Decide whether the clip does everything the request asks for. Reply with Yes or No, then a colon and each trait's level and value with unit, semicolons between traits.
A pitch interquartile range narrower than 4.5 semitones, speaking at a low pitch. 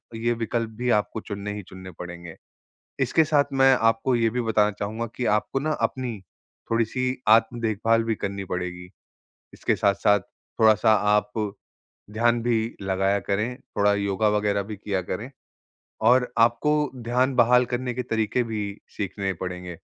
Yes: average, 3.1 semitones; low, 110 Hz